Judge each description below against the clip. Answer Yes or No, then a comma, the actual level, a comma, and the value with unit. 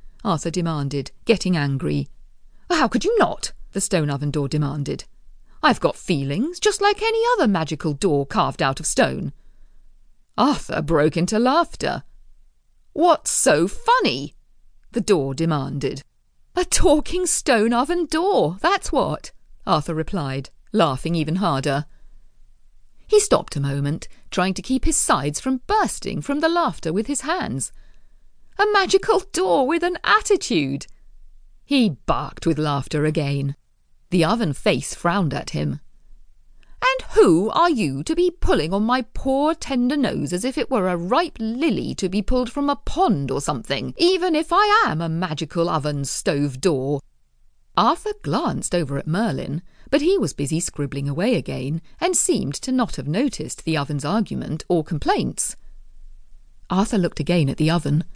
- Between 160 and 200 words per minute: No, average, 150 wpm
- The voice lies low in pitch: No, medium, 185 Hz